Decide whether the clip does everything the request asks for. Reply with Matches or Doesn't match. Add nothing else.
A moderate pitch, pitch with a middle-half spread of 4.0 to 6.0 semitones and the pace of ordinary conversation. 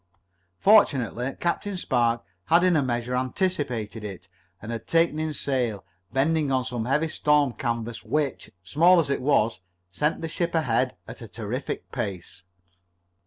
Doesn't match